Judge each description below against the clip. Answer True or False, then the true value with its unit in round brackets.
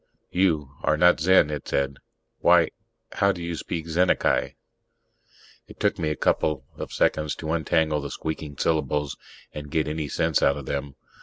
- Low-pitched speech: True (75 Hz)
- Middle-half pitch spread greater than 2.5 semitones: False (2.2 semitones)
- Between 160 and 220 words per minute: True (165 wpm)